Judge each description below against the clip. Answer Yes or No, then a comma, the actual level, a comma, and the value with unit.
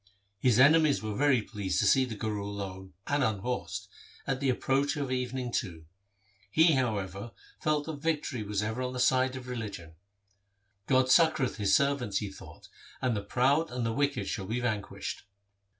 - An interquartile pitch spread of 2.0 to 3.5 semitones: No, average, 4.8 semitones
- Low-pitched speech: Yes, low, 125 Hz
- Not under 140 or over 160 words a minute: No, average, 180 wpm